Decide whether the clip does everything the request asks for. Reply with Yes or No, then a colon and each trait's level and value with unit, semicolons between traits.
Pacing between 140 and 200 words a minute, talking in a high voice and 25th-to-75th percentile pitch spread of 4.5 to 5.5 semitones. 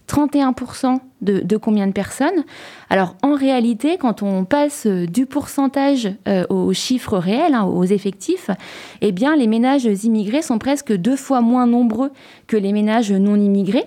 Yes: average, 160 wpm; high, 240 Hz; average, 5.2 semitones